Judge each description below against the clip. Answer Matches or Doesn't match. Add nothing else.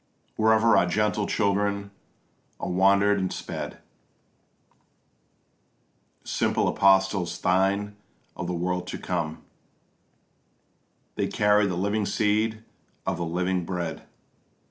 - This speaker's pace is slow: Matches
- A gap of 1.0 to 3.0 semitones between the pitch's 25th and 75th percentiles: Matches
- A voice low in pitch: Matches